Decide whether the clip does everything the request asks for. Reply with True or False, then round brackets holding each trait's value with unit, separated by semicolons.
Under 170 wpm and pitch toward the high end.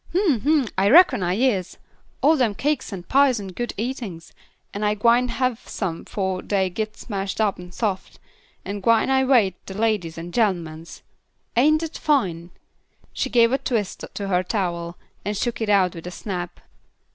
False (180 wpm; 210 Hz)